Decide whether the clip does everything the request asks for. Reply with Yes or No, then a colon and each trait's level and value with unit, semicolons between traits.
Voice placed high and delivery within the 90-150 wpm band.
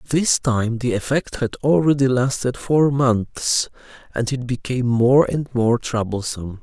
No: low, 125 Hz; average, 145 wpm